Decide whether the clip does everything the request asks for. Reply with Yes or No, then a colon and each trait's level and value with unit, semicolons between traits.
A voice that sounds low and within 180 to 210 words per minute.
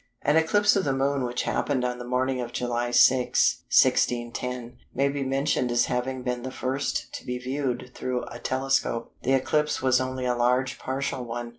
Yes: low, 130 Hz; average, 185 wpm